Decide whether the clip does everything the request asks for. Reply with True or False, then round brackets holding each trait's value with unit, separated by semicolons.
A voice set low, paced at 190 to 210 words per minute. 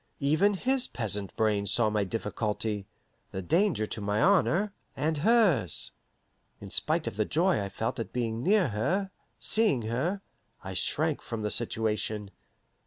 False (115 Hz; 150 wpm)